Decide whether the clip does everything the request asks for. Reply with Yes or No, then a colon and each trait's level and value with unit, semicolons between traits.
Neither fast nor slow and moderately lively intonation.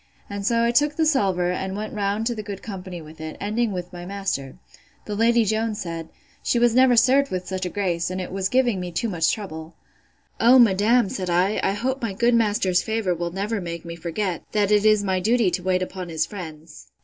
No: fast, 225 wpm; average, 4.1 semitones